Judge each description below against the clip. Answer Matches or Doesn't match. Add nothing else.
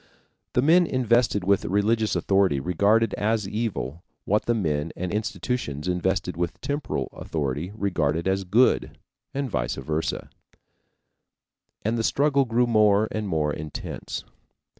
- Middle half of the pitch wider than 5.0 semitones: Matches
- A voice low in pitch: Matches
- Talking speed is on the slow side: Matches